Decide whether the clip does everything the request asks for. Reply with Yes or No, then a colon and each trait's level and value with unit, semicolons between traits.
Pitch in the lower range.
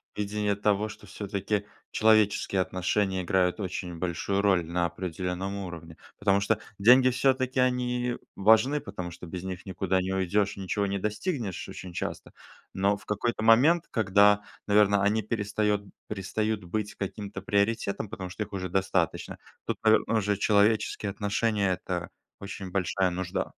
Yes: low, 100 Hz